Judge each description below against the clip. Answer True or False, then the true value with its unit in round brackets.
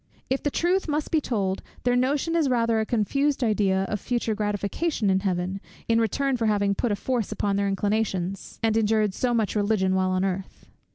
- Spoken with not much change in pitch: False (4.0 semitones)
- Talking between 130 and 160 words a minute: False (195 wpm)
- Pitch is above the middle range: True (215 Hz)